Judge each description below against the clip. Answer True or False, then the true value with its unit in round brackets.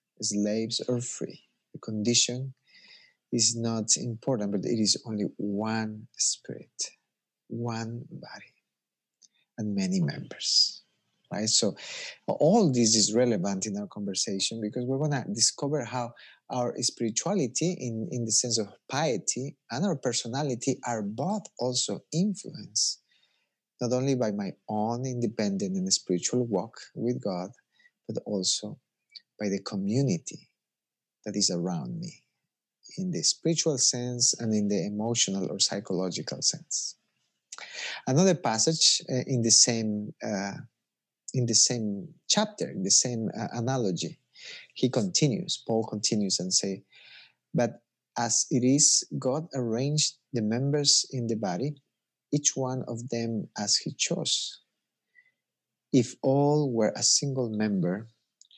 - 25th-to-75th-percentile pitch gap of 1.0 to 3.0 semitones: False (4.9 semitones)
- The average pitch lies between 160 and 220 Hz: False (120 Hz)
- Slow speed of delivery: True (130 wpm)